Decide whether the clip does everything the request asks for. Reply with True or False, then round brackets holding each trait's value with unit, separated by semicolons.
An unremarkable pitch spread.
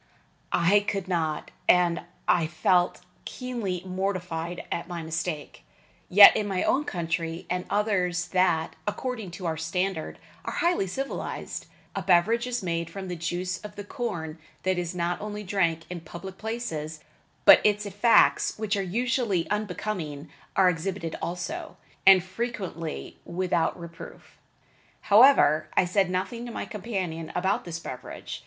True (3.4 semitones)